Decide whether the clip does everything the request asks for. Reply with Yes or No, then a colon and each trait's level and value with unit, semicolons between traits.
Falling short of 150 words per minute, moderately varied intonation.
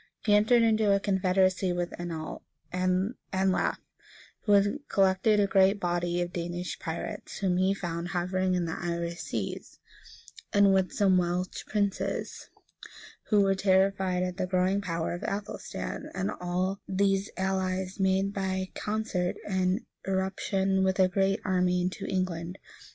No: average, 140 wpm; narrow, 1.5 semitones